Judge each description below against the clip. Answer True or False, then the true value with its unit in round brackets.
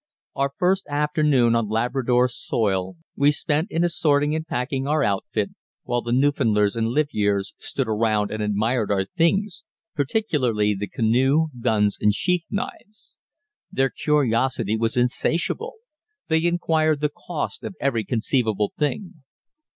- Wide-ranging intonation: True (5.7 semitones)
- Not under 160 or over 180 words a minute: False (135 wpm)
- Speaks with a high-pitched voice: False (130 Hz)